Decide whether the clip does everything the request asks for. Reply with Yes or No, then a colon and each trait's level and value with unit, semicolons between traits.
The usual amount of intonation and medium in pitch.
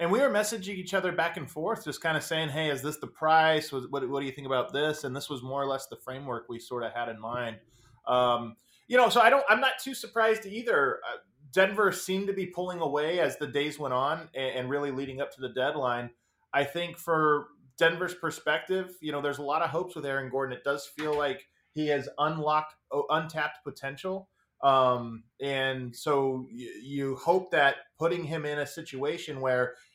Yes: average, 3.8 semitones; medium, 145 Hz